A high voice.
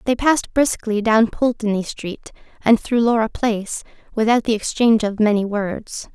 Yes: high, 220 Hz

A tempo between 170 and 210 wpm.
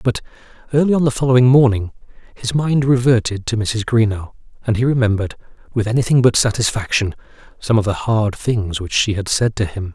Yes: average, 180 wpm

